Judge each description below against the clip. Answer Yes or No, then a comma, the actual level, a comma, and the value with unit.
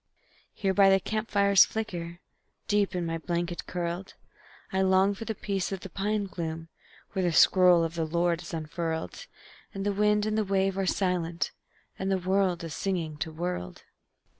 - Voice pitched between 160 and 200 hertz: Yes, medium, 185 Hz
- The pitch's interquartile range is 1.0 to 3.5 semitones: Yes, narrow, 2.6 semitones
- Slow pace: No, average, 175 wpm